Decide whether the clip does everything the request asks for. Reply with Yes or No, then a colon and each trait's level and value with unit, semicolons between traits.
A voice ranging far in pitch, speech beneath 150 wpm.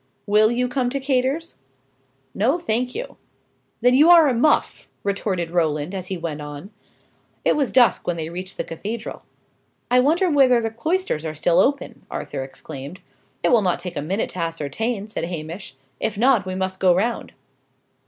No: wide, 6.8 semitones; average, 175 wpm